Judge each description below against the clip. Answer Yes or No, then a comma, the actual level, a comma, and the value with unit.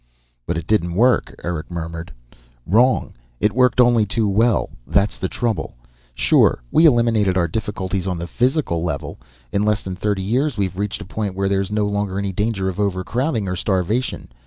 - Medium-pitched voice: No, low, 100 Hz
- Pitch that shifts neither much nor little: Yes, average, 3.5 semitones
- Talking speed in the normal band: Yes, average, 180 wpm